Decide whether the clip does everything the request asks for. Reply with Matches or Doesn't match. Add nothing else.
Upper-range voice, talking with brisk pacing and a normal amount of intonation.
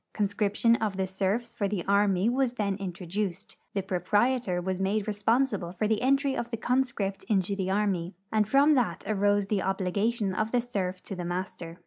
Doesn't match